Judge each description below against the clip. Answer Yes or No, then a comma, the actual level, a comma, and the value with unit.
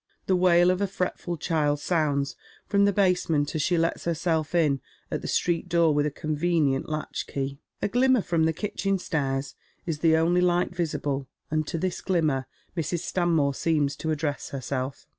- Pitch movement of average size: Yes, average, 3.3 semitones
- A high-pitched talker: No, medium, 160 Hz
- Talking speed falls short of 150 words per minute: No, average, 180 wpm